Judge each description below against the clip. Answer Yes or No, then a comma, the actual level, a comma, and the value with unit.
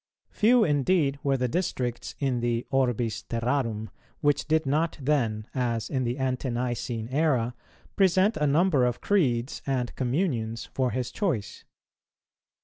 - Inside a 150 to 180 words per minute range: No, average, 140 wpm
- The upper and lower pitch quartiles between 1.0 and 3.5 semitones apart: No, average, 4.0 semitones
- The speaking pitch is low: Yes, low, 130 Hz